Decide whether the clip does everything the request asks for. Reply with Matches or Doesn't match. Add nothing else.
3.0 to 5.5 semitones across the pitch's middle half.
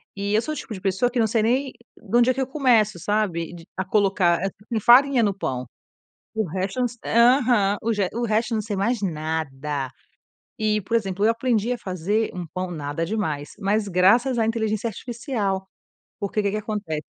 Matches